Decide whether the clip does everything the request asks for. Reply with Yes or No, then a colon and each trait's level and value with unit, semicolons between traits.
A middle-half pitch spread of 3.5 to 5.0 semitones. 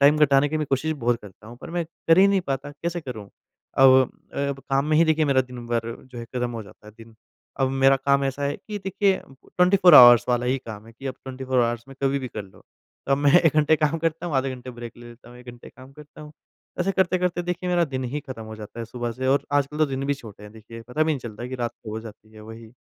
Yes: average, 4.2 semitones